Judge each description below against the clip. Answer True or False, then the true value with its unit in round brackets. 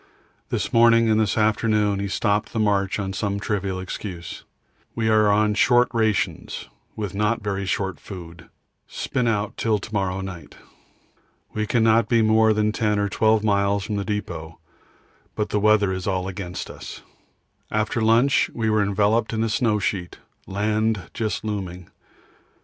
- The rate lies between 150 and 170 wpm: True (160 wpm)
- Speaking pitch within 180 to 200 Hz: False (105 Hz)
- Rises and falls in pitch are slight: True (2.0 semitones)